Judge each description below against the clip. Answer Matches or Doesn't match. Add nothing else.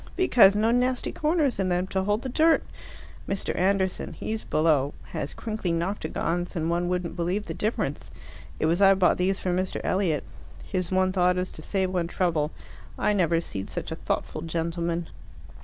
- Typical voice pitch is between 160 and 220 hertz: Matches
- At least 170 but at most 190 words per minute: Matches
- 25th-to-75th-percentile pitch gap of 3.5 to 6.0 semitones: Doesn't match